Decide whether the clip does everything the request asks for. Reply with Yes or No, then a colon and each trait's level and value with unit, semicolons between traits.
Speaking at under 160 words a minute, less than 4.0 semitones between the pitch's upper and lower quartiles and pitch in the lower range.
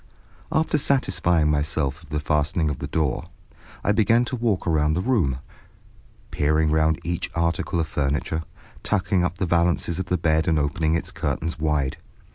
No: average, 165 wpm; average, 2.9 semitones; very low, 80 Hz